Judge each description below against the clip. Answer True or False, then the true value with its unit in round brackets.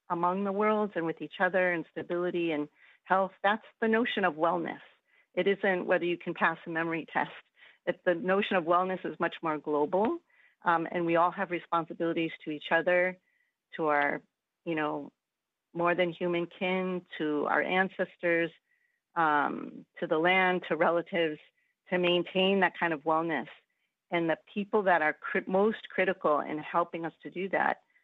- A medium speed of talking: True (170 wpm)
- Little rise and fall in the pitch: True (2.2 semitones)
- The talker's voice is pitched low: False (175 Hz)